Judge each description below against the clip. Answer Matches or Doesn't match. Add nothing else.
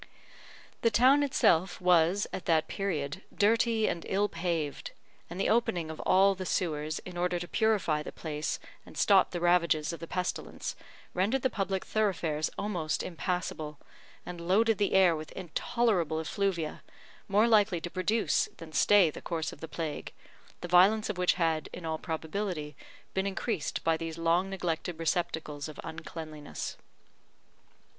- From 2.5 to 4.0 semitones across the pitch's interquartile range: Matches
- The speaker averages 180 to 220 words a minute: Doesn't match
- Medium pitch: Matches